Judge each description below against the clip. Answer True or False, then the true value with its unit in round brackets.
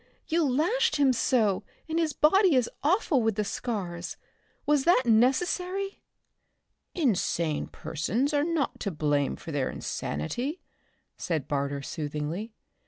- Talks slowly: True (125 wpm)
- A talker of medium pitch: False (245 Hz)